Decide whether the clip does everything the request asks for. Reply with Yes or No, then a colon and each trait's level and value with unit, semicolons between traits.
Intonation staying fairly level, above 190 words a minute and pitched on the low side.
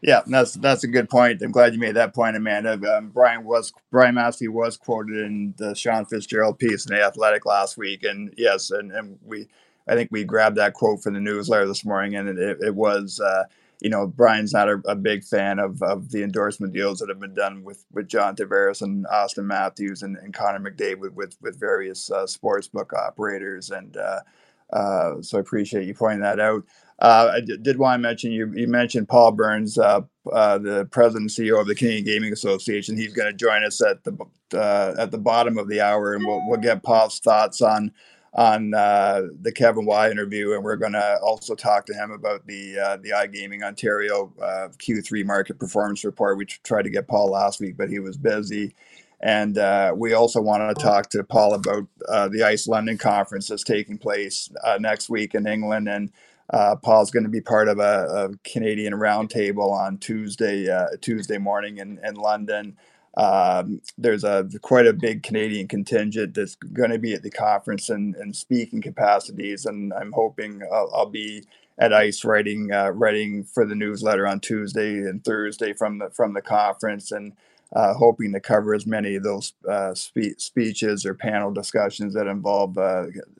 Yes: narrow, 1.9 semitones; average, 200 wpm; low, 105 Hz